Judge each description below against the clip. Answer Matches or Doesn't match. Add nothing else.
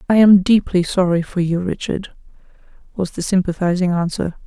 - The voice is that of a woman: Matches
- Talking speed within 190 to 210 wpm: Doesn't match